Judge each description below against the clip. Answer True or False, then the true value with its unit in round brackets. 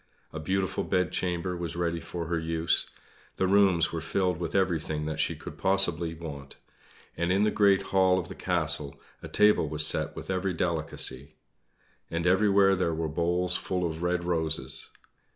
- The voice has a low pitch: True (85 Hz)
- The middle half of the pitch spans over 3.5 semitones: False (2.5 semitones)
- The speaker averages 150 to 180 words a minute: True (170 wpm)